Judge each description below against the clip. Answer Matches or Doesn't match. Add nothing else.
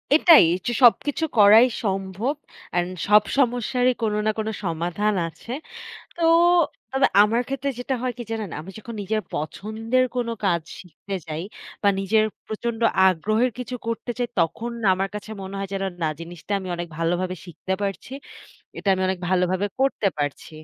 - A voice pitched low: Doesn't match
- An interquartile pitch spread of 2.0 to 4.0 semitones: Doesn't match